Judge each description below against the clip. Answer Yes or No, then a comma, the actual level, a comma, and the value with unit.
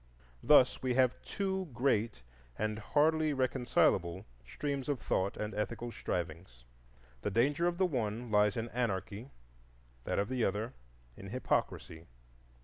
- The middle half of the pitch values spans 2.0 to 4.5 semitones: No, average, 4.9 semitones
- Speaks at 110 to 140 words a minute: Yes, slow, 135 wpm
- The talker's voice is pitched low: Yes, low, 120 Hz